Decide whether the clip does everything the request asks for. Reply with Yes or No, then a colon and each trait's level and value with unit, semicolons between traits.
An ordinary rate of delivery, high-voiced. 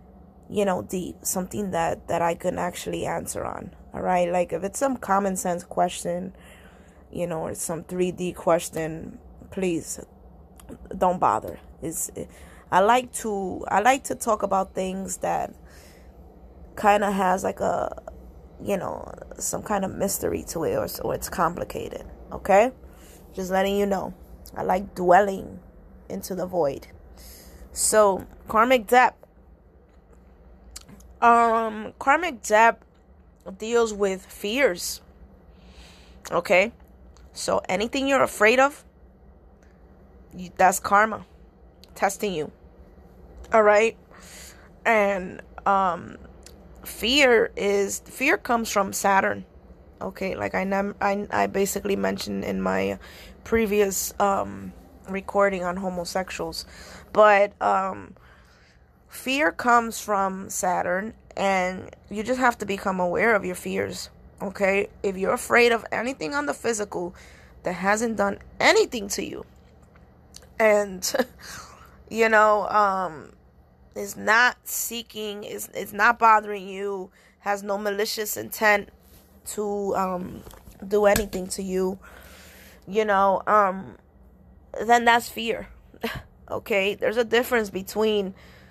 No: slow, 120 wpm; high, 195 Hz